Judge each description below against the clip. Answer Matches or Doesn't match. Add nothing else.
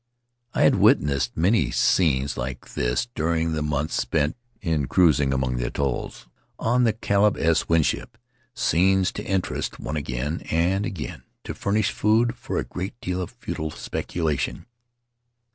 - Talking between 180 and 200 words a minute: Doesn't match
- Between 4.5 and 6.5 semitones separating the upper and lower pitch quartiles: Matches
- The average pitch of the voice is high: Doesn't match